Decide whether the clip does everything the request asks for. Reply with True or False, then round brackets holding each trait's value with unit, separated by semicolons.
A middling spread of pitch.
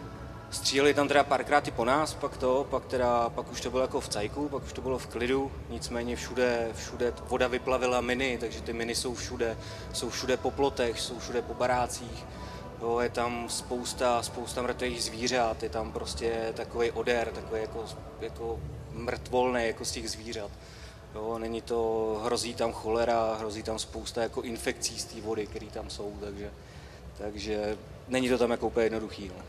False (2.1 semitones)